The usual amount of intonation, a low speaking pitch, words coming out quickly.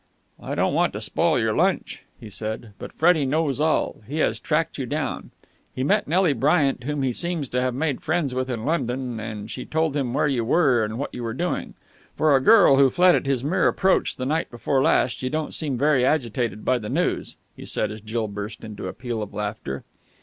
Yes: average, 4.6 semitones; low, 130 Hz; fast, 225 wpm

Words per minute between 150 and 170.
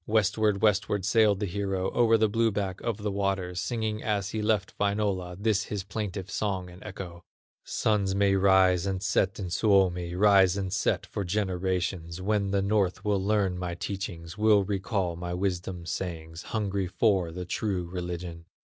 Yes: average, 165 wpm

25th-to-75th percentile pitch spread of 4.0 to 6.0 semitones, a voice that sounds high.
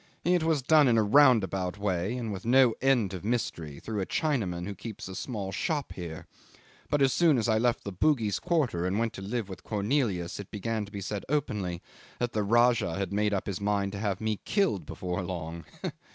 No: average, 4.5 semitones; low, 105 Hz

